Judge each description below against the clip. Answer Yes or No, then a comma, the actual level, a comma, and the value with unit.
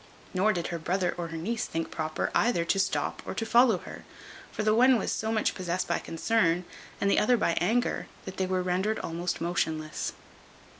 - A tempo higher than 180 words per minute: Yes, average, 200 wpm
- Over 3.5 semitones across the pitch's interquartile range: Yes, average, 4.3 semitones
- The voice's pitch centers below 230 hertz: Yes, medium, 185 Hz